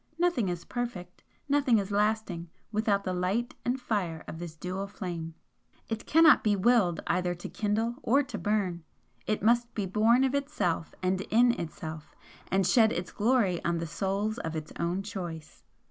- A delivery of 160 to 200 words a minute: Yes, average, 170 wpm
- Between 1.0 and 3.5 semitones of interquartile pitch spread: No, average, 4.9 semitones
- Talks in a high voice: Yes, high, 200 Hz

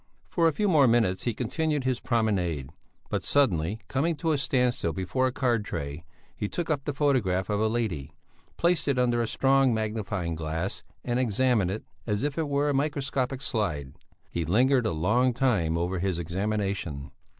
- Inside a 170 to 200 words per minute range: Yes, average, 180 wpm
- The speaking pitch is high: No, low, 115 Hz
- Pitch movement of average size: No, wide, 6.7 semitones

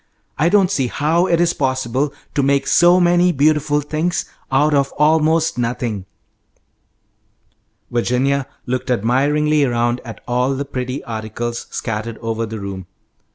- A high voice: No, low, 135 Hz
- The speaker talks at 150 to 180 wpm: No, slow, 135 wpm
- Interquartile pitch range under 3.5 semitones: No, average, 4.3 semitones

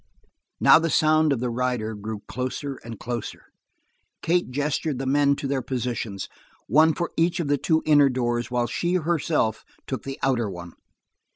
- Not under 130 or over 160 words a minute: No, average, 170 wpm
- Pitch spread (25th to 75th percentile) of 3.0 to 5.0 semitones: Yes, average, 4.4 semitones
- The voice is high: No, low, 135 Hz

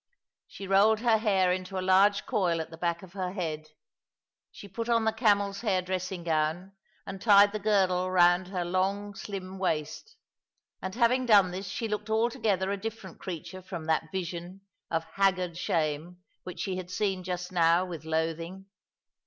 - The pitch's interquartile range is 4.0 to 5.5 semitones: No, narrow, 2.5 semitones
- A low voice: No, medium, 185 Hz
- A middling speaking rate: Yes, average, 170 wpm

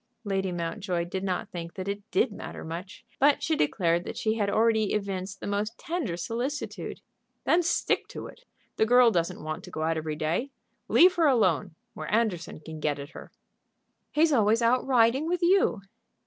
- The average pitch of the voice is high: Yes, high, 205 Hz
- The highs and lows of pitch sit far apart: Yes, wide, 6.3 semitones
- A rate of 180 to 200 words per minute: Yes, average, 185 wpm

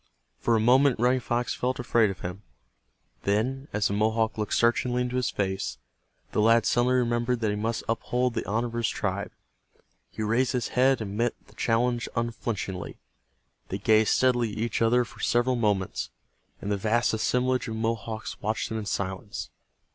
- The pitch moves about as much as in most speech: No, narrow, 2.3 semitones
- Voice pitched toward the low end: Yes, low, 115 Hz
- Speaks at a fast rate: No, average, 180 wpm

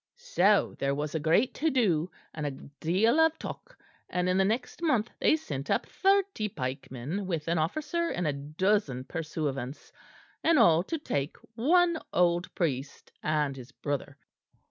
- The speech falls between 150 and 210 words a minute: Yes, average, 160 wpm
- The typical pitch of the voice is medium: Yes, medium, 170 Hz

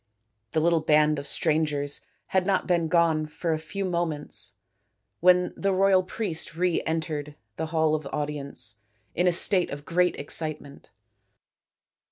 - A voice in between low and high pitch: Yes, medium, 160 Hz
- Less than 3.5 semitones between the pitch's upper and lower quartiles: Yes, average, 3.0 semitones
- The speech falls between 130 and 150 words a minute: Yes, average, 145 wpm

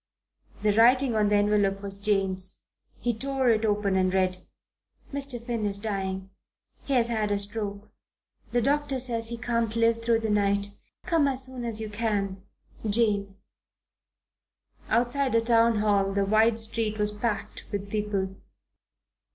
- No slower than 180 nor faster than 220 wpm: No, average, 150 wpm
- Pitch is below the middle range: No, high, 215 Hz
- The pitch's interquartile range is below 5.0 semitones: Yes, narrow, 2.6 semitones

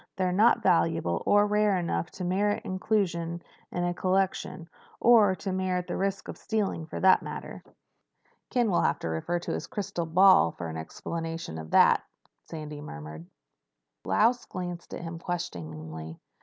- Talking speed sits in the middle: Yes, average, 155 wpm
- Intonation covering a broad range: No, average, 4.2 semitones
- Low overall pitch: No, medium, 175 Hz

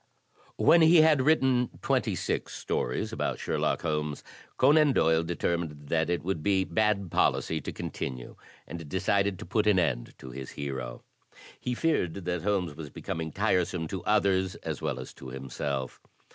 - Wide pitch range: Yes, wide, 5.9 semitones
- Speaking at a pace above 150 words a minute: Yes, average, 160 wpm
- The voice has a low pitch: Yes, very low, 85 Hz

